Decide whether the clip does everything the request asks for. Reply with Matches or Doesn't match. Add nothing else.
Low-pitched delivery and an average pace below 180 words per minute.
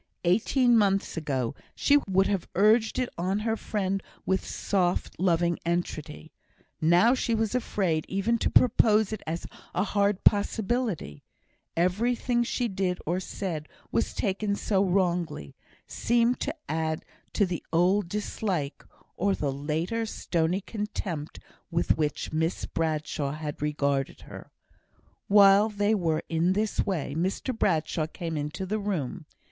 Doesn't match